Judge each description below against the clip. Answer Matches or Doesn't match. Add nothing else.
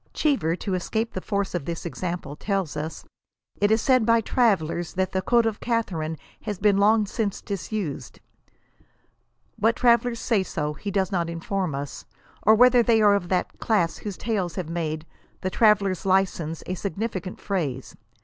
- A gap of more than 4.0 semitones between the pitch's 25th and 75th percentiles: Matches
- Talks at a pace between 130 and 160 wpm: Doesn't match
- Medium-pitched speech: Doesn't match